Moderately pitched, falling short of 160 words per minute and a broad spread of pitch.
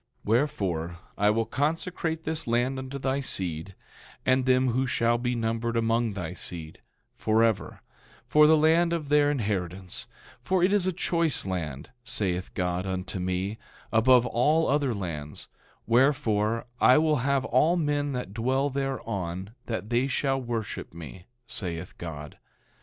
No: low, 120 Hz; average, 145 wpm; wide, 6.6 semitones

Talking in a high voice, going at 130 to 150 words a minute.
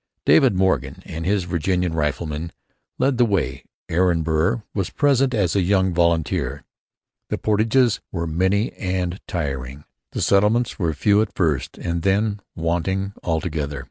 No: very low, 90 Hz; average, 140 wpm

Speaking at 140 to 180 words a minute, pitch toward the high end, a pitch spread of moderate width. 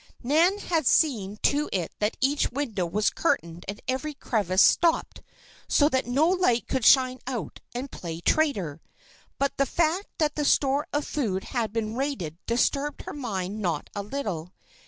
No: average, 165 wpm; very high, 255 Hz; wide, 6.4 semitones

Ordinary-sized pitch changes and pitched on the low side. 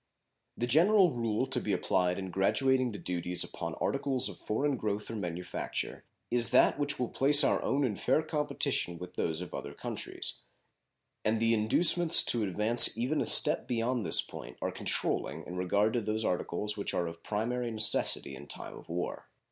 No: wide, 5.9 semitones; low, 110 Hz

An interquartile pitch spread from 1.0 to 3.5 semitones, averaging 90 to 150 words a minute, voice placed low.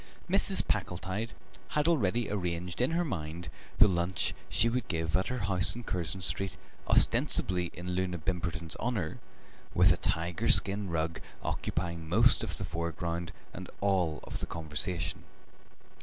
Yes: average, 2.8 semitones; average, 145 wpm; very low, 90 Hz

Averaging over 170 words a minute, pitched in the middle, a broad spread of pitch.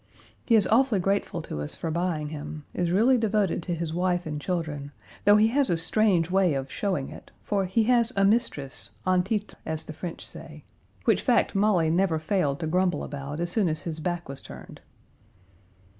No: average, 195 wpm; medium, 180 Hz; average, 4.5 semitones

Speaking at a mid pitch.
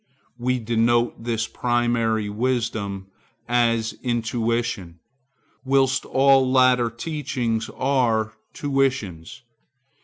No: low, 120 Hz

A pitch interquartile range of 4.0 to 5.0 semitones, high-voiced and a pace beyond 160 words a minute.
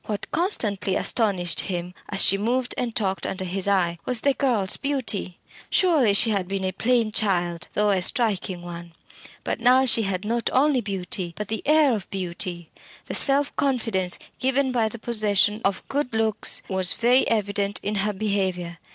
Yes: average, 4.4 semitones; high, 210 Hz; average, 175 wpm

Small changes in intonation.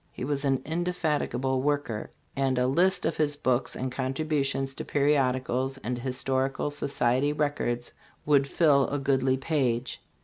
Yes: narrow, 2.1 semitones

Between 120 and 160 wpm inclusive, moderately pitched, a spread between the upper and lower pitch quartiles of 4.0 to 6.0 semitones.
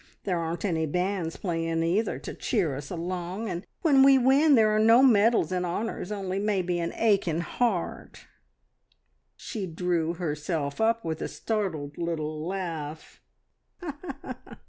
Yes: average, 140 wpm; medium, 180 Hz; average, 4.6 semitones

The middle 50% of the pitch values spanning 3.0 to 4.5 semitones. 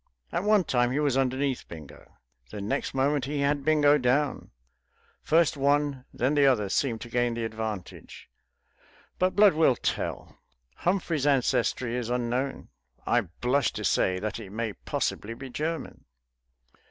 Yes: average, 3.9 semitones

